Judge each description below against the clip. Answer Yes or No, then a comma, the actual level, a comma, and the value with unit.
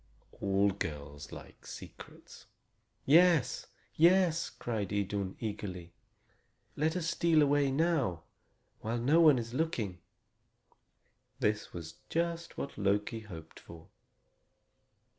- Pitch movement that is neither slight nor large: No, wide, 8.6 semitones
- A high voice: No, low, 115 Hz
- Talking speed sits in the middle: No, slow, 105 wpm